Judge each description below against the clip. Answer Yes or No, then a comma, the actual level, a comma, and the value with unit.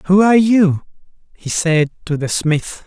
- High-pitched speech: No, medium, 175 Hz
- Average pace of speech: Yes, average, 170 wpm